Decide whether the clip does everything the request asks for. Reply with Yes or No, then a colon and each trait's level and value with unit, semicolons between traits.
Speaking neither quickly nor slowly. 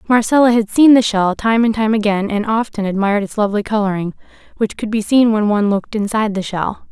No: fast, 215 wpm